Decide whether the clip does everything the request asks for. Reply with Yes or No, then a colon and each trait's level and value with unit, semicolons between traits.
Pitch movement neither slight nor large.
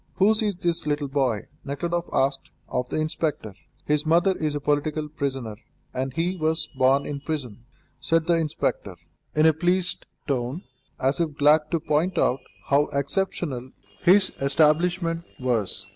Yes: average, 3.5 semitones